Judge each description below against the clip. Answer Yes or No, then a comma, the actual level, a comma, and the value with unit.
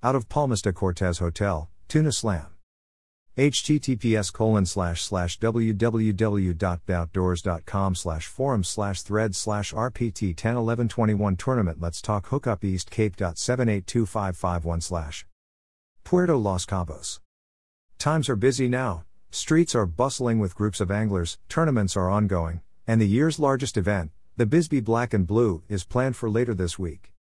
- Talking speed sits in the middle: No, slow, 125 wpm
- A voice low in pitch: Yes, low, 100 Hz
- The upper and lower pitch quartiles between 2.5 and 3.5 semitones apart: No, average, 5.0 semitones